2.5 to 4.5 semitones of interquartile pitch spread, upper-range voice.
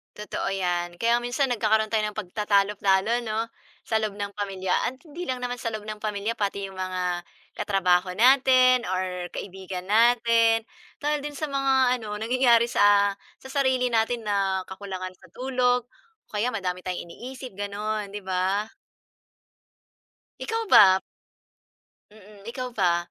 Yes: average, 4.2 semitones; high, 210 Hz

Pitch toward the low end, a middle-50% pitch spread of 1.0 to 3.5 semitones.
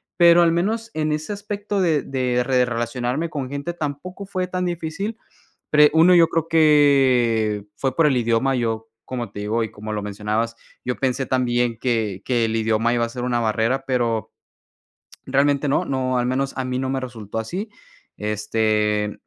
No: low, 130 Hz; average, 5.2 semitones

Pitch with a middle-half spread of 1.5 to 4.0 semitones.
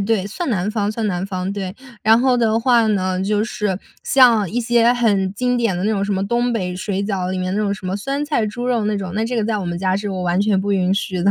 Yes: average, 3.3 semitones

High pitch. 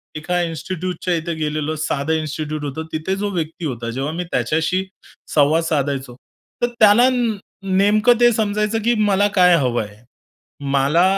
No: medium, 160 Hz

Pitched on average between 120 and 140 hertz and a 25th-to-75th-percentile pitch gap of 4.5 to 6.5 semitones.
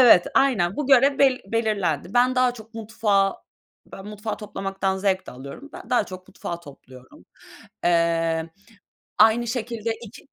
No: high, 210 Hz; average, 5.3 semitones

